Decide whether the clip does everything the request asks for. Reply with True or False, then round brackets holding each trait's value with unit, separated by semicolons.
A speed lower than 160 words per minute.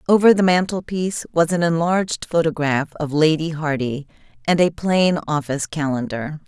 True (140 wpm)